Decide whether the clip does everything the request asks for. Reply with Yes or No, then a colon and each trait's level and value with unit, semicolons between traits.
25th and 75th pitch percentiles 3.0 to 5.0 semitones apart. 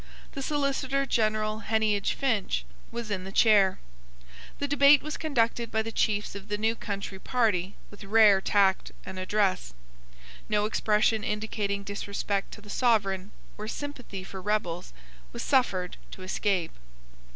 No: narrow, 2.6 semitones